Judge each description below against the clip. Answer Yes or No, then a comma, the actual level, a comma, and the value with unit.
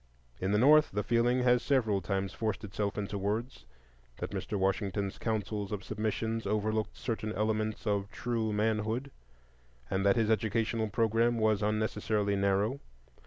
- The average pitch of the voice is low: Yes, low, 110 Hz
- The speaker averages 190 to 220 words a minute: No, average, 145 wpm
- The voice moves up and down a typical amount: No, narrow, 1.9 semitones